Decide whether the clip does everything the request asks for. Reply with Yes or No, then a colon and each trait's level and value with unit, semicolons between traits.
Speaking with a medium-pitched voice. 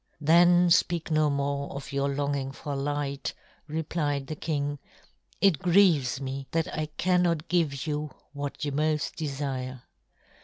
Yes: medium, 145 Hz